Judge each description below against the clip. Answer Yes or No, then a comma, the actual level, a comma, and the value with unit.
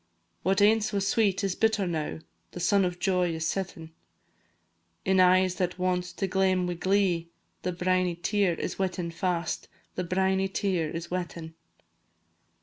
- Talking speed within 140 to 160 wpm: Yes, average, 150 wpm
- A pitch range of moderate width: No, narrow, 1.8 semitones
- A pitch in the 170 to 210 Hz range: Yes, medium, 185 Hz